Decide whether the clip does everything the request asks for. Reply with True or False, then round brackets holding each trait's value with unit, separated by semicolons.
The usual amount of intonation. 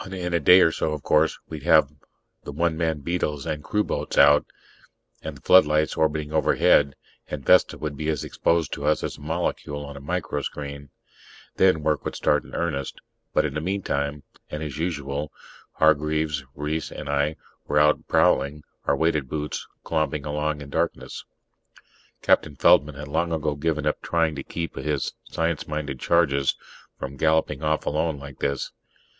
False (1.8 semitones)